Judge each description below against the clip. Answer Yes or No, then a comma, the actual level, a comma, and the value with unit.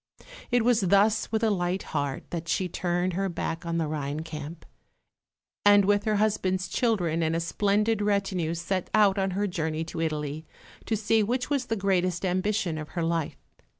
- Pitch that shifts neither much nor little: Yes, average, 3.9 semitones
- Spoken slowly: No, average, 185 wpm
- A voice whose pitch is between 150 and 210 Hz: Yes, medium, 185 Hz